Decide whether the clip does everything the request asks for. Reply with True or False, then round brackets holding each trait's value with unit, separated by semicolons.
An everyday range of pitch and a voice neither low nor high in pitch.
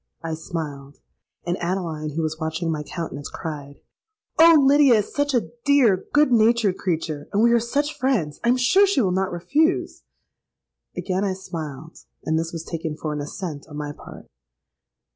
False (7.1 semitones; 175 Hz)